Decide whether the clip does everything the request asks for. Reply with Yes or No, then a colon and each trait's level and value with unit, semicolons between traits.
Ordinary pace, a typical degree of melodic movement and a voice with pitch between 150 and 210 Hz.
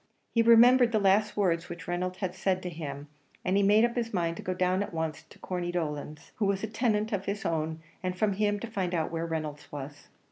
No: fast, 235 wpm; average, 4.0 semitones; medium, 185 Hz